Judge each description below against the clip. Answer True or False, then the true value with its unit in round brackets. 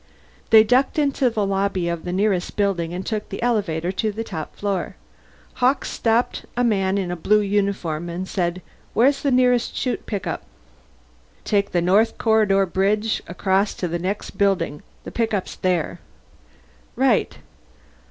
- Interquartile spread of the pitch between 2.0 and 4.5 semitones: True (3.5 semitones)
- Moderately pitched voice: False (200 Hz)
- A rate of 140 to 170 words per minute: True (150 wpm)